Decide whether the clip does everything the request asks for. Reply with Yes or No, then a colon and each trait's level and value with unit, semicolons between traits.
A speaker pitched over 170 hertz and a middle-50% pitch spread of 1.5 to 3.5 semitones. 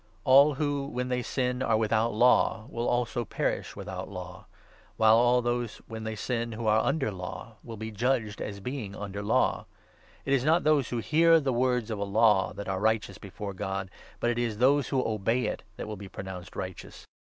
No: low, 115 Hz; average, 3.2 semitones